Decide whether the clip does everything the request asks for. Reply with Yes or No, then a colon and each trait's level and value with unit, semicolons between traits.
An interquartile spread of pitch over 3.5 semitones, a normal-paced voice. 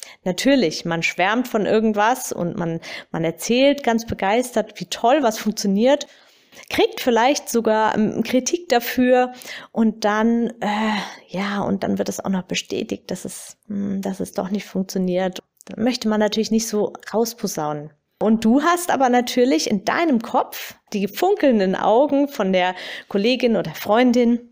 Yes: average, 4.1 semitones; average, 150 wpm